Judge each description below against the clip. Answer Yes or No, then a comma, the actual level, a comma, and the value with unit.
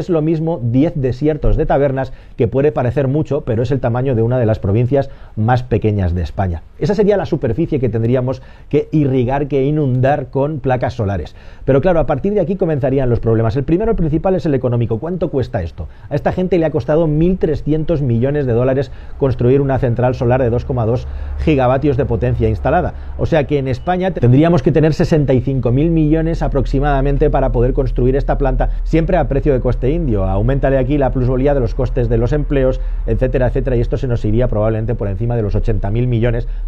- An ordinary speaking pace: No, fast, 200 wpm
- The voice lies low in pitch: Yes, low, 130 Hz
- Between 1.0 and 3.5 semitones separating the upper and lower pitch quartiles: No, average, 3.9 semitones